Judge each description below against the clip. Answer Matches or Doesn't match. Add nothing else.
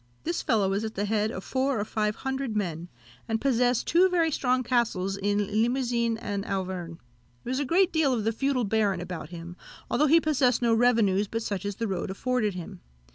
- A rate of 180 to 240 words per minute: Matches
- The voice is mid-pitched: Doesn't match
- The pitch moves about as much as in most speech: Matches